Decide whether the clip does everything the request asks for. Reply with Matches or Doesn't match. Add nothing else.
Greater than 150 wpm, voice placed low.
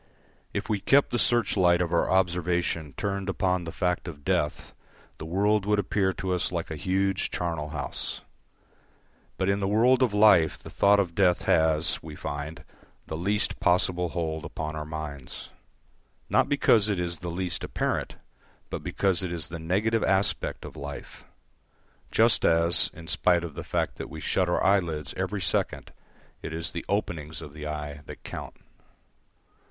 Matches